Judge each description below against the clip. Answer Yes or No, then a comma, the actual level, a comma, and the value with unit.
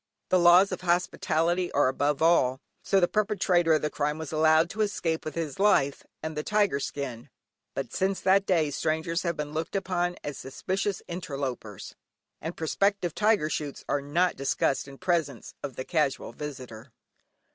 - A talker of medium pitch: Yes, medium, 160 Hz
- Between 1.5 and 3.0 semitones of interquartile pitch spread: No, average, 4.1 semitones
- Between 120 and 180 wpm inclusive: Yes, average, 170 wpm